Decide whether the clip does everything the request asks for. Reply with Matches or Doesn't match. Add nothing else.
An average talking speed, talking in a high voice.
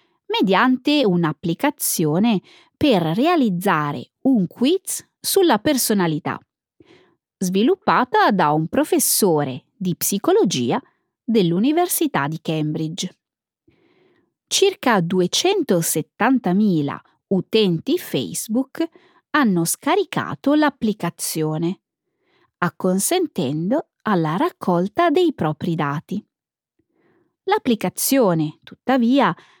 Doesn't match